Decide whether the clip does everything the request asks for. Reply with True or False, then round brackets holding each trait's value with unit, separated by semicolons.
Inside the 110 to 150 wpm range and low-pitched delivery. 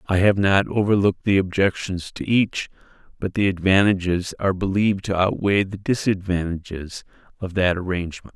True (145 wpm; 95 Hz)